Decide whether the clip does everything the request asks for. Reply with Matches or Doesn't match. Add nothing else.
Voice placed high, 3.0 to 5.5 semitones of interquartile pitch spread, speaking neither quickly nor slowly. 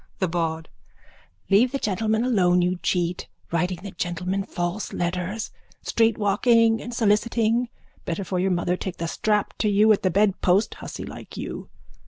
Matches